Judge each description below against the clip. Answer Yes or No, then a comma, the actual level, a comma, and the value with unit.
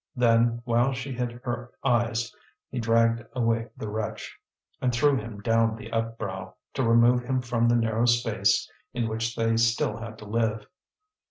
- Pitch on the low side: Yes, low, 115 Hz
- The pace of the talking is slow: No, average, 165 wpm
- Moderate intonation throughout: No, narrow, 1.1 semitones